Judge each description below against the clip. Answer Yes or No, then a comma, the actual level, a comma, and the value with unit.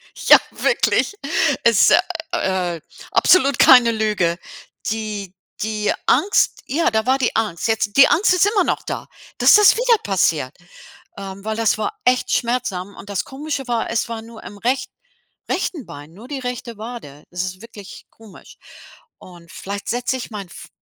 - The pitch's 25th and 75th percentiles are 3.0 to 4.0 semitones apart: No, average, 4.5 semitones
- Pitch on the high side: Yes, high, 220 Hz